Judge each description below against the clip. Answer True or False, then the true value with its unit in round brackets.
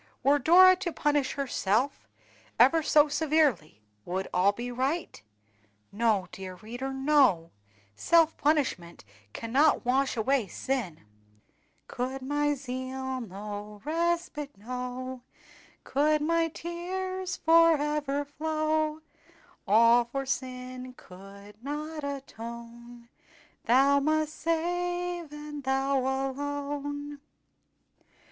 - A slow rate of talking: True (95 wpm)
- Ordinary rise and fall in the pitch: True (4.3 semitones)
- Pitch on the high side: True (275 Hz)